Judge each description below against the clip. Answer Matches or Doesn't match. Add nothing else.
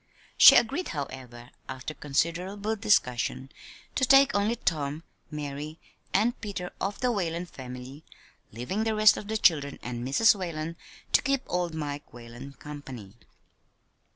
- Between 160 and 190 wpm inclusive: Doesn't match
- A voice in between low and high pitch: Matches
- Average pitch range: Doesn't match